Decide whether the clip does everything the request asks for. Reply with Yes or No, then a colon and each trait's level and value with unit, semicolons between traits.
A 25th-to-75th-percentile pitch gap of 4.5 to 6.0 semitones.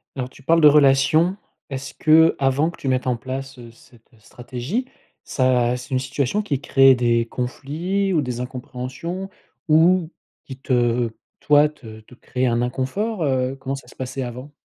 No: average, 3.4 semitones